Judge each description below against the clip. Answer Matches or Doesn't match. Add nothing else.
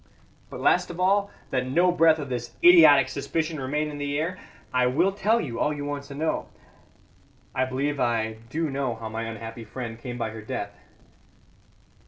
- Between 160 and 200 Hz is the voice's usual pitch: Doesn't match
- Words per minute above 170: Matches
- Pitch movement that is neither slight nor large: Matches